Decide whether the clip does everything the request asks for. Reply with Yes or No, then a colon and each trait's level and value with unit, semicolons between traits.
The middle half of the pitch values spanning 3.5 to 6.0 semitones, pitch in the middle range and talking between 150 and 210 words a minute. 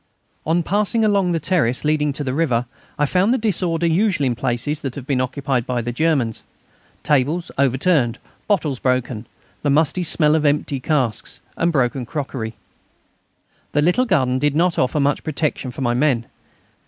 Yes: average, 4.5 semitones; medium, 145 Hz; average, 165 wpm